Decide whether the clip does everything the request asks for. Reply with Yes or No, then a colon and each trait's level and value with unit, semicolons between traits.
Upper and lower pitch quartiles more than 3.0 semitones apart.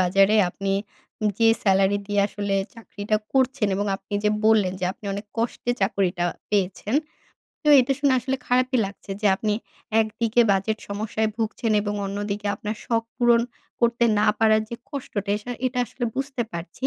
No: average, 2.7 semitones